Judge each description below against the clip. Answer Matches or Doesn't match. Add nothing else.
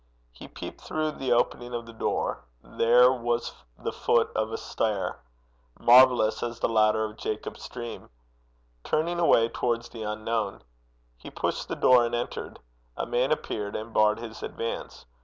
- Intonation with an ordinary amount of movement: Doesn't match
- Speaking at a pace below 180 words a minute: Matches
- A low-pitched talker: Matches